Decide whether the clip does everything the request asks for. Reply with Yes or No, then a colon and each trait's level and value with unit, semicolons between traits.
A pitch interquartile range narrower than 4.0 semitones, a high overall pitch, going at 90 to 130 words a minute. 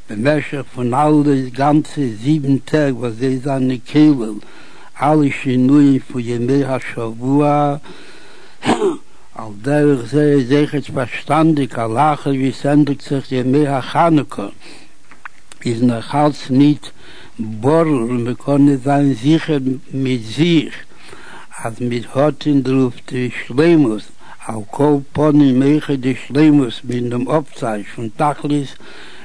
No: average, 2.9 semitones; medium, 140 Hz; average, 120 wpm